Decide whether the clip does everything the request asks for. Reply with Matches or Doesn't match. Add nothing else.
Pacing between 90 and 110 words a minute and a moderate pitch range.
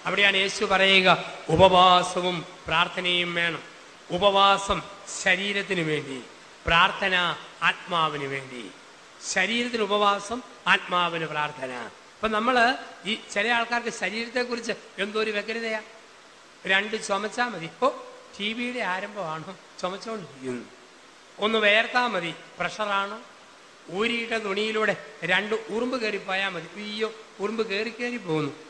Matches